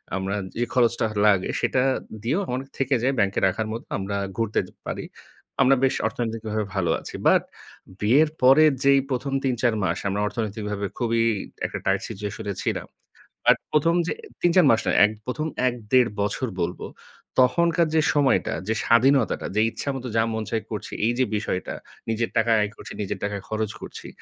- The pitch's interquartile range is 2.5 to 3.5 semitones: No, average, 4.2 semitones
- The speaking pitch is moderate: No, low, 115 Hz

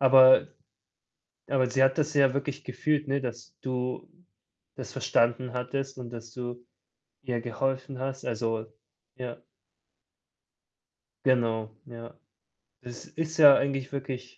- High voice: No, low, 130 Hz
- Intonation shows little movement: Yes, narrow, 2.0 semitones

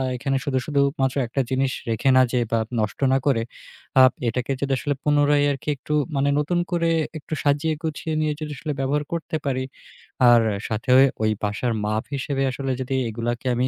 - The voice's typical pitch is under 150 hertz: Yes, low, 135 Hz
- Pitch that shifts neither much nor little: Yes, average, 3.2 semitones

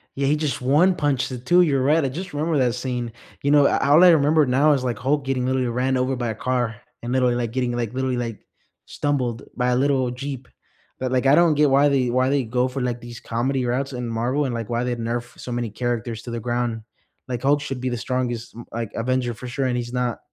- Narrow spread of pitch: Yes, narrow, 2.3 semitones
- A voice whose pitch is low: Yes, low, 125 Hz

